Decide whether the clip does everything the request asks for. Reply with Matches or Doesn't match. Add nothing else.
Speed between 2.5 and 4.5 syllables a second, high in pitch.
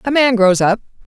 Doesn't match